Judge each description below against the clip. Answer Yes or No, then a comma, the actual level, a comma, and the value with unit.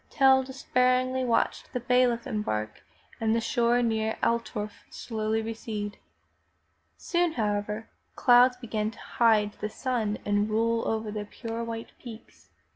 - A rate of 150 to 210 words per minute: No, slow, 135 wpm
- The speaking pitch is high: Yes, high, 225 Hz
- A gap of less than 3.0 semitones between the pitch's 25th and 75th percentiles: Yes, narrow, 2.6 semitones